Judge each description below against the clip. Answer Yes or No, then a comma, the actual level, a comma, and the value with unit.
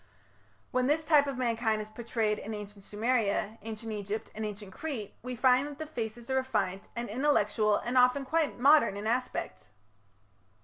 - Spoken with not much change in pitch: No, average, 3.7 semitones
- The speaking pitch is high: Yes, high, 230 Hz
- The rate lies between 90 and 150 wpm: No, average, 170 wpm